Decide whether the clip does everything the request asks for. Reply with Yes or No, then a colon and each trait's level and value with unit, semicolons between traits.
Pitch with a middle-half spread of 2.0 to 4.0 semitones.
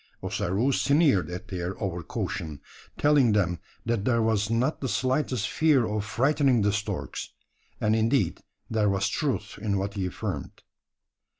No: average, 4.6 semitones